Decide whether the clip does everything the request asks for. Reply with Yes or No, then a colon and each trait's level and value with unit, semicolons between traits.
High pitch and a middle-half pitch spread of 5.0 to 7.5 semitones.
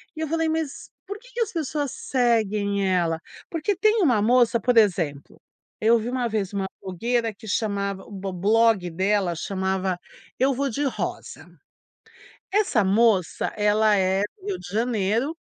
Yes: high, 220 Hz; wide, 5.4 semitones